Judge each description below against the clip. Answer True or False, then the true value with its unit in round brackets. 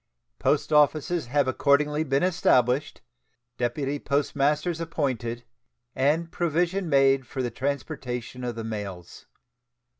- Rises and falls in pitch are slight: False (3.7 semitones)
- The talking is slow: True (110 wpm)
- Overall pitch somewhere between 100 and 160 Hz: True (140 Hz)